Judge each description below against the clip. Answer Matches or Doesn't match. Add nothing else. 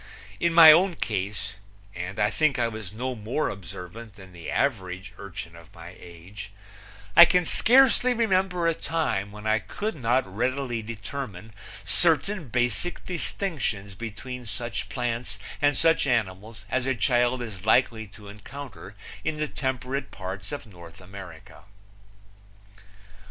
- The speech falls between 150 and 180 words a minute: Doesn't match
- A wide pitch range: Matches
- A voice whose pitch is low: Matches